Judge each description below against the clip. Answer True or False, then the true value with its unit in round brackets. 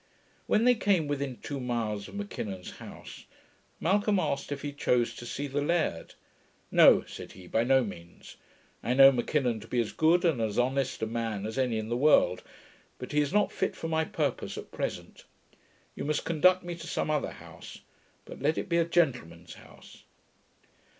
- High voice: False (135 Hz)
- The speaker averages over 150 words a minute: True (190 wpm)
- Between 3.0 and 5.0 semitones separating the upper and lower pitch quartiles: False (5.6 semitones)